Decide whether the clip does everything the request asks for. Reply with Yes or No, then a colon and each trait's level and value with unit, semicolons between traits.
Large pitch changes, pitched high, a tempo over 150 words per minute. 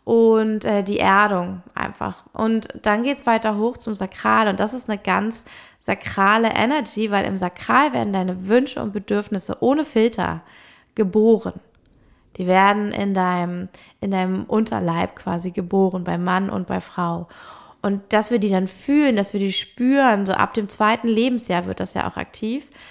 No: average, 3.2 semitones; high, 205 Hz; average, 170 wpm